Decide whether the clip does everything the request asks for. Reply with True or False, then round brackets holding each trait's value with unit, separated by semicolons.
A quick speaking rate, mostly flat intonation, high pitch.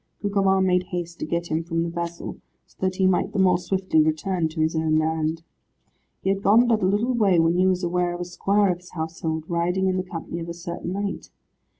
False (235 wpm; 2.3 semitones; 175 Hz)